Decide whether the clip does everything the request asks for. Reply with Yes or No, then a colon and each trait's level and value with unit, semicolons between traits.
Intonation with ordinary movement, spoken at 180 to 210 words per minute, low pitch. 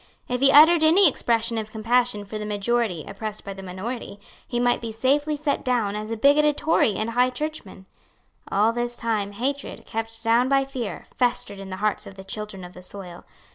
No: average, 3.8 semitones; average, 200 wpm; high, 230 Hz